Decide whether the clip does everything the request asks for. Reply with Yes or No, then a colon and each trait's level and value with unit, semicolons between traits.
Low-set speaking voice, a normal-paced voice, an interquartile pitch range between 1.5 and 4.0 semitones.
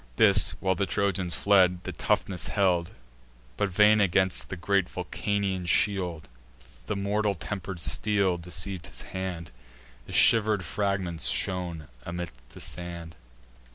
No: very low, 95 Hz; slow, 125 wpm; narrow, 2.4 semitones